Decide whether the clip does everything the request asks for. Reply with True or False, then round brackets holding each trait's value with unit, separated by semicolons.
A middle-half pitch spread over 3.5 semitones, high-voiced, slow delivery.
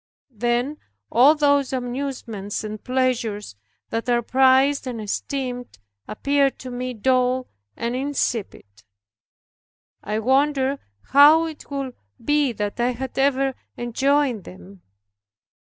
False (2.8 semitones; 255 Hz; 110 wpm)